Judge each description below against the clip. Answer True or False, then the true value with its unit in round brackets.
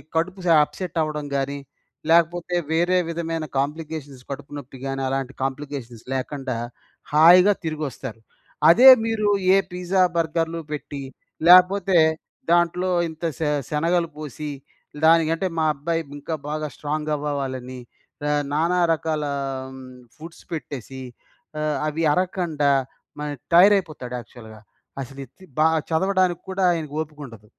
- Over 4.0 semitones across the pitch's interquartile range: False (3.5 semitones)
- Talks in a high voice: False (155 Hz)